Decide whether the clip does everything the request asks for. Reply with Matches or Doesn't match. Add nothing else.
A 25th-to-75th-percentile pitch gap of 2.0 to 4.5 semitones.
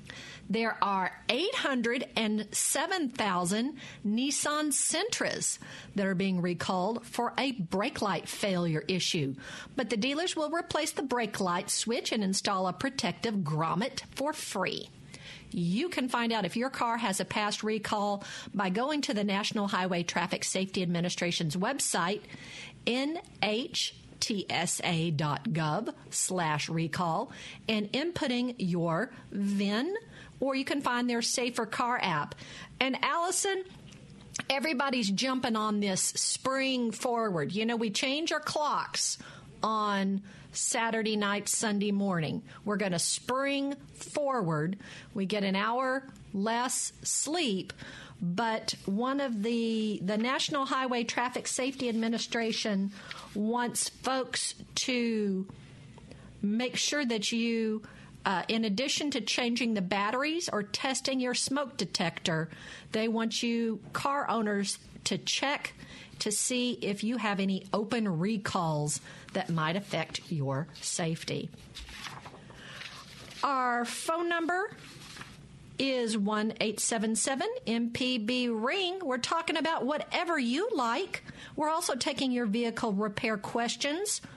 Doesn't match